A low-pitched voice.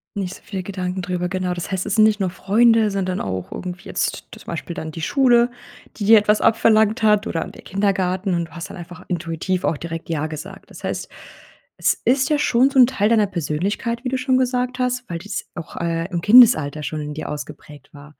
No: high, 190 Hz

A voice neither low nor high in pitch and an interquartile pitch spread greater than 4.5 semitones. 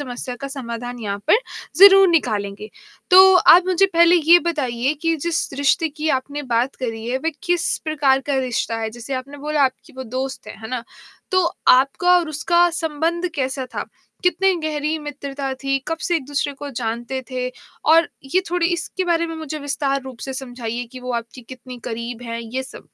No: very high, 275 Hz; average, 4.9 semitones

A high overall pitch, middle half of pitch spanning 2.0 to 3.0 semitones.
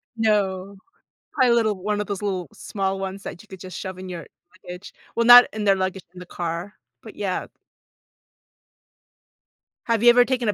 Yes: high, 195 Hz; average, 2.7 semitones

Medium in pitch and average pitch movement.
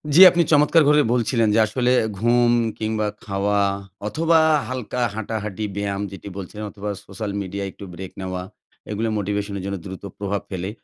No: low, 105 Hz; average, 3.2 semitones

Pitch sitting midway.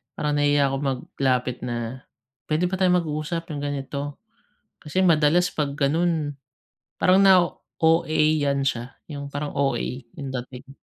Yes: medium, 145 Hz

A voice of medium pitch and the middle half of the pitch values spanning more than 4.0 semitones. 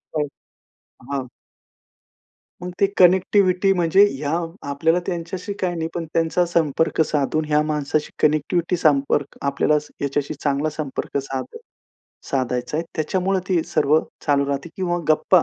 No: medium, 155 Hz; average, 3.7 semitones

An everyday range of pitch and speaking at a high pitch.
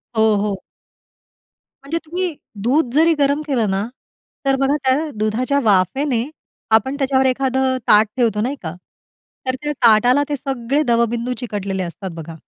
Yes: average, 4.4 semitones; very high, 250 Hz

